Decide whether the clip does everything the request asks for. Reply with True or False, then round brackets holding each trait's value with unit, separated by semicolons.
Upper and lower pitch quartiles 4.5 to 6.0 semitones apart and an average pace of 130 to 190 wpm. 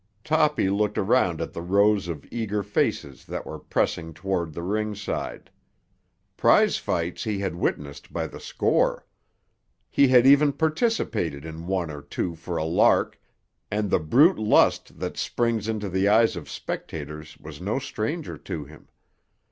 True (5.1 semitones; 155 wpm)